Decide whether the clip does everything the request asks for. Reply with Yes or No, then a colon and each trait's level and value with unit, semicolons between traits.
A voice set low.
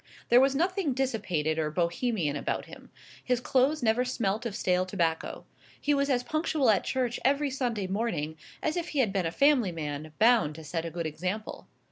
No: high, 225 Hz